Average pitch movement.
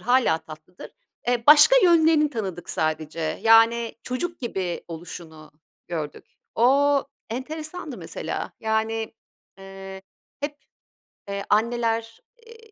No: wide, 7.8 semitones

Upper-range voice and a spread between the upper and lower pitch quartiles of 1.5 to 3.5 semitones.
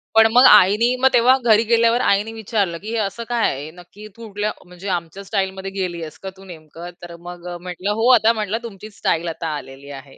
No: high, 195 Hz; average, 4.3 semitones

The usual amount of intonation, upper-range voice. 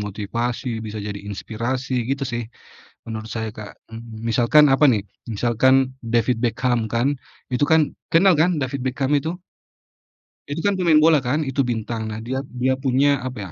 No: average, 3.6 semitones; low, 125 Hz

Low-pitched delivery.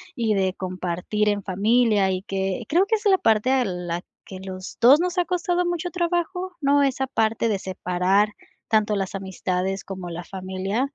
No: high, 210 Hz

